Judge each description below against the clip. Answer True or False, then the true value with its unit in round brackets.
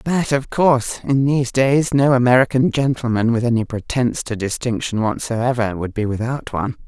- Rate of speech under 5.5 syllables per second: True (5.3 syllables/s)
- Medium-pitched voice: False (125 Hz)